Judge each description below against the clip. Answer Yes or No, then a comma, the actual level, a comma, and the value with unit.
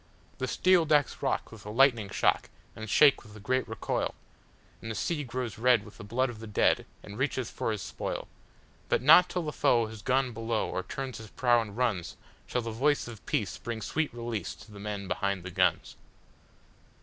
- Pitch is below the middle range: Yes, low, 115 Hz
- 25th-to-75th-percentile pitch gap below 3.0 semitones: No, average, 3.5 semitones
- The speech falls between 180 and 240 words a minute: Yes, average, 195 wpm